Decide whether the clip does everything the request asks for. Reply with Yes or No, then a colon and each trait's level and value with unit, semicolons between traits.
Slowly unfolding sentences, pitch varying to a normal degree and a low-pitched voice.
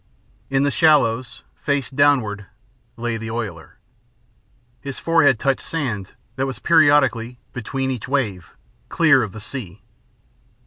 Yes: slow, 125 wpm; average, 4.1 semitones; low, 130 Hz